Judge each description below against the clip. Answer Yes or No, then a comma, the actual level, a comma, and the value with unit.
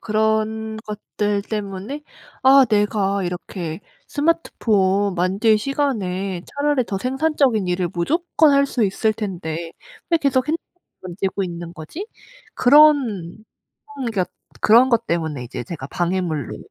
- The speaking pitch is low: No, high, 210 Hz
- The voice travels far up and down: Yes, wide, 6.3 semitones